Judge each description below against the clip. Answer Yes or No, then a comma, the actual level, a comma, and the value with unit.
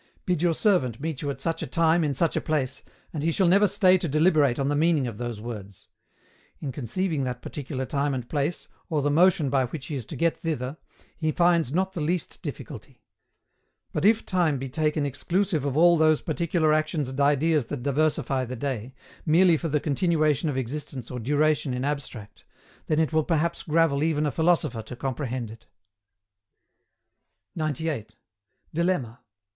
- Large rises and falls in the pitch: No, average, 3.9 semitones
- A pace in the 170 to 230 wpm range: Yes, average, 180 wpm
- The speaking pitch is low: No, medium, 150 Hz